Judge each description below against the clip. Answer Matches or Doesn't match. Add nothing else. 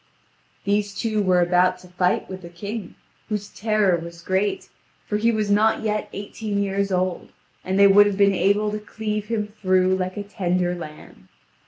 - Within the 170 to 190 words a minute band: Matches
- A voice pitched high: Matches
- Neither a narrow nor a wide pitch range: Doesn't match